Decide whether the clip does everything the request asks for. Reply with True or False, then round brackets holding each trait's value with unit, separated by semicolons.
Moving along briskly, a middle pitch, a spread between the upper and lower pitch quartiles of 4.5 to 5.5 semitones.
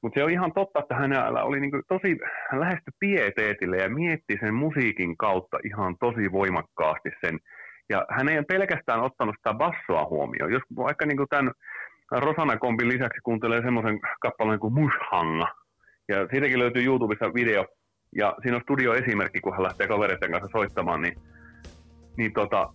False (160 wpm; 120 Hz; 5.1 semitones)